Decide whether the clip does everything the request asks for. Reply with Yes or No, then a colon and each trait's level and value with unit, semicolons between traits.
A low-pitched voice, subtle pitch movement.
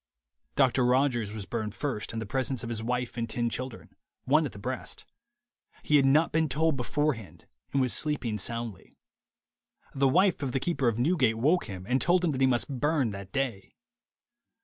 No: low, 130 Hz; average, 3.9 semitones